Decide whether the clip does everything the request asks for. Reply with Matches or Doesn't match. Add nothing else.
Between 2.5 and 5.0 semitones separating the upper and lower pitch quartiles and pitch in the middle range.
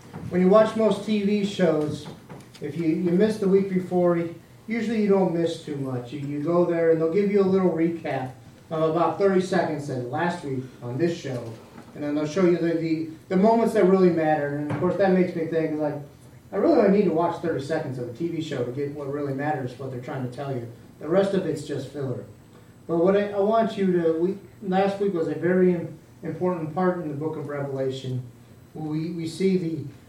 Matches